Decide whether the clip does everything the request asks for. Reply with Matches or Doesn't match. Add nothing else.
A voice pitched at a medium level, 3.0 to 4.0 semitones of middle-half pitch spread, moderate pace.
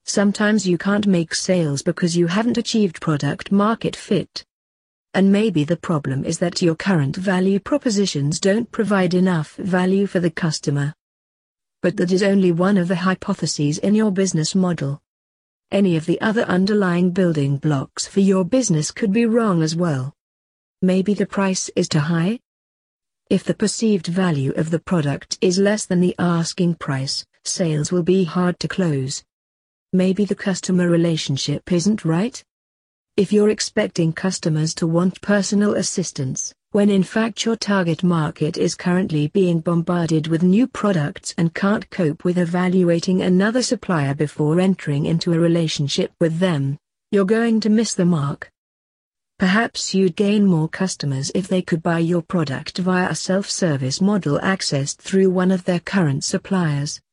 Matches